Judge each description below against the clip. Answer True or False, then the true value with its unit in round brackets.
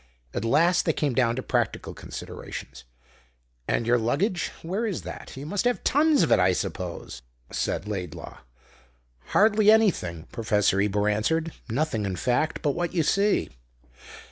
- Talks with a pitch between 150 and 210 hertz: False (140 Hz)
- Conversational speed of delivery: True (150 wpm)